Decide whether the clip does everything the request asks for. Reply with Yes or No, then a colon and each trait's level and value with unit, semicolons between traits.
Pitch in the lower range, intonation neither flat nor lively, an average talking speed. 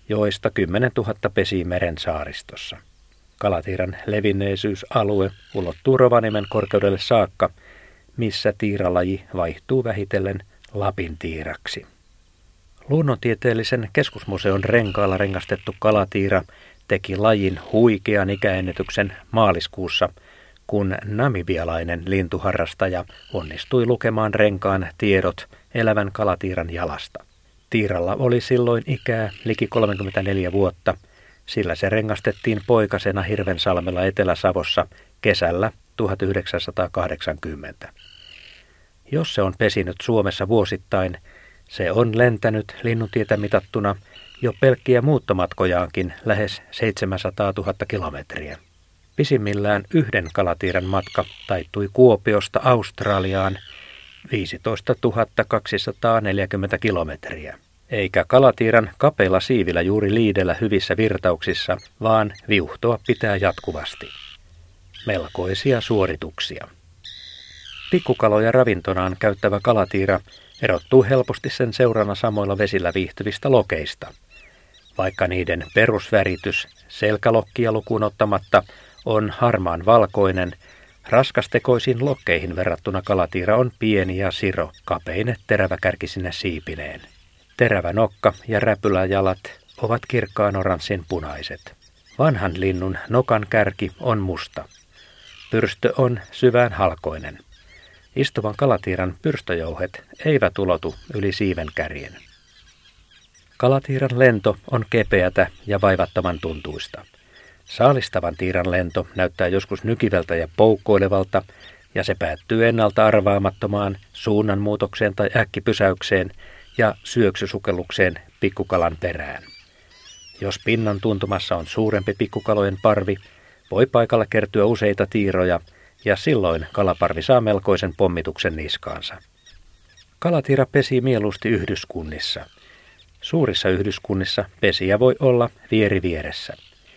No: low, 100 Hz; average, 3.3 semitones; slow, 90 wpm